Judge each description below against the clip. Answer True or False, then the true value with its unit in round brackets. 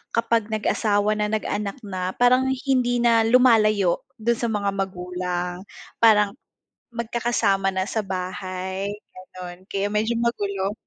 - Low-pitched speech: False (210 Hz)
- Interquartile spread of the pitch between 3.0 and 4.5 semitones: True (3.5 semitones)